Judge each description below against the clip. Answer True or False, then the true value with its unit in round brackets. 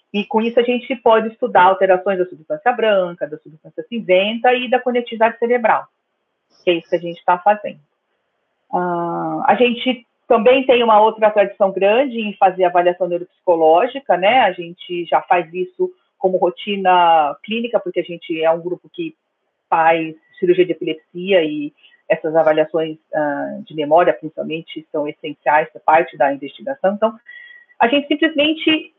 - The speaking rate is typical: True (160 wpm)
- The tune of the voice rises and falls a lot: True (6.3 semitones)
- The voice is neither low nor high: False (195 Hz)